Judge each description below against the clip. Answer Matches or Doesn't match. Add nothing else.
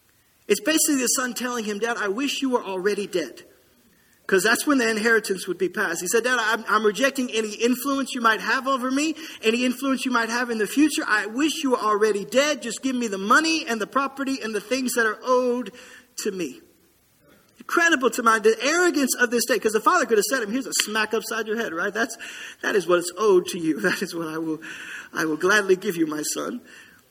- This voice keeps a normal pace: Doesn't match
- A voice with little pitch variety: Doesn't match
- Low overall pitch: Doesn't match